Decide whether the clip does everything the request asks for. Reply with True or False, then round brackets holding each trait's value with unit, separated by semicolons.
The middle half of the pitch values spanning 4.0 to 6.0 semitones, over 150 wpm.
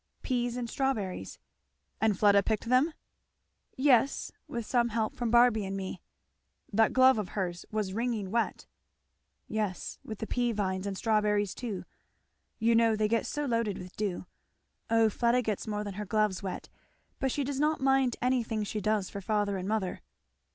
False (3.1 semitones; 170 wpm)